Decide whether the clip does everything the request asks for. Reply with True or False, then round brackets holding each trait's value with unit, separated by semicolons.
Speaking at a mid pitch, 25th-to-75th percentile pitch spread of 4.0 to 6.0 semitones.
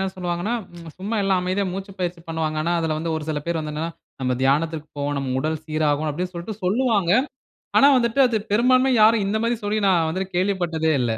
True (175 Hz; 4.4 semitones)